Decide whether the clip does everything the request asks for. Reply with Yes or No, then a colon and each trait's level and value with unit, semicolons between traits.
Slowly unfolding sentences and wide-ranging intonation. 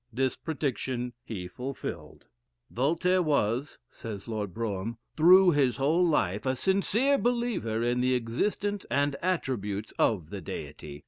Yes: slow, 130 wpm; wide, 7.5 semitones